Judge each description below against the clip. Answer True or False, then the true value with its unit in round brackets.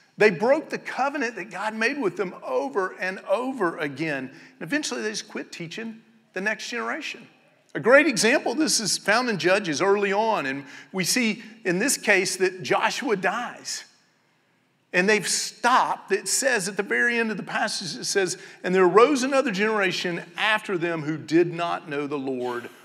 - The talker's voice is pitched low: False (210 Hz)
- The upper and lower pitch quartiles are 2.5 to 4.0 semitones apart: False (4.4 semitones)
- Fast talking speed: False (180 wpm)